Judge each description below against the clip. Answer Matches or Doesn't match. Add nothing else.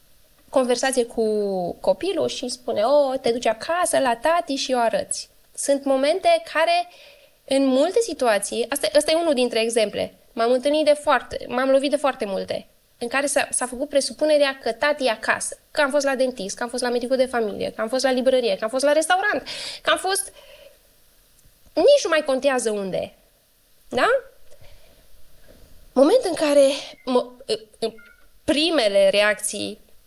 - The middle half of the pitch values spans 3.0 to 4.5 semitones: Matches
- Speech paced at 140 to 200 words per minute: Matches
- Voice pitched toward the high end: Matches